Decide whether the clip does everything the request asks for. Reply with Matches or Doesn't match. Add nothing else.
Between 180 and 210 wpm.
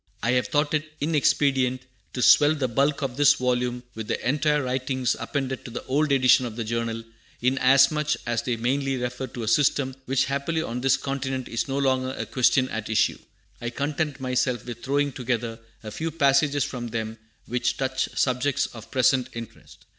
Matches